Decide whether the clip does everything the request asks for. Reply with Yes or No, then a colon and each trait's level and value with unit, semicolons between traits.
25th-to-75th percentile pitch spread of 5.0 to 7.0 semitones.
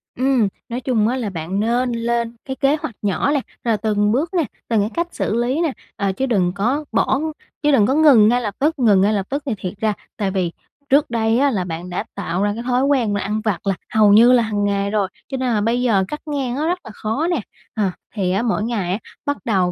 No: average, 4.5 semitones